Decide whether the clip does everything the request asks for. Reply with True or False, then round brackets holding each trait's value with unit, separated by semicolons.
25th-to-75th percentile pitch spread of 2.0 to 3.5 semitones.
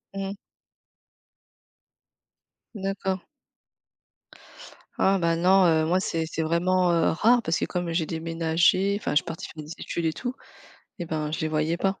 True (2.9 semitones)